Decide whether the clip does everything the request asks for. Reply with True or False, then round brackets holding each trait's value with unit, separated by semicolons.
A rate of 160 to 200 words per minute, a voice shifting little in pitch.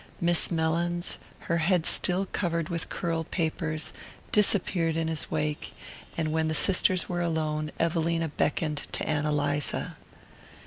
False (135 wpm; 1.9 semitones)